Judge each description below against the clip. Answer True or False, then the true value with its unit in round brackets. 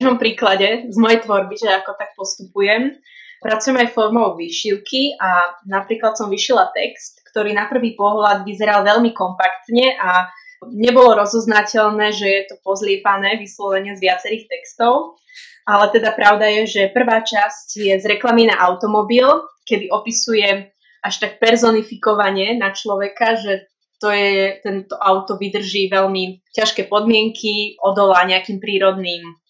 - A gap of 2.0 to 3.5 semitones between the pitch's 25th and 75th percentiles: True (2.5 semitones)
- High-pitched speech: True (210 Hz)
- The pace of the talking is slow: False (135 wpm)